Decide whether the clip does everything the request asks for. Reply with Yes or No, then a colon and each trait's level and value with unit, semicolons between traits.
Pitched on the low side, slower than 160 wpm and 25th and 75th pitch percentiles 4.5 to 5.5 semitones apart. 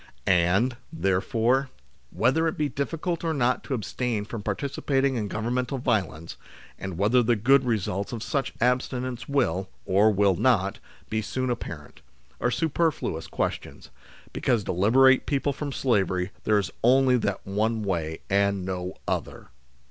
Yes: low, 115 Hz; average, 145 wpm; average, 5.1 semitones